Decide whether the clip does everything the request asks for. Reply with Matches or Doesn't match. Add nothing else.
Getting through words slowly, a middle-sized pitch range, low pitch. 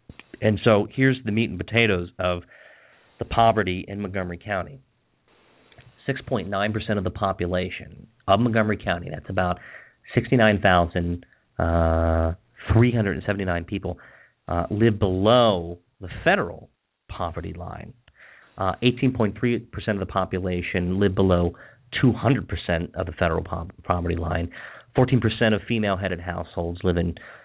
Matches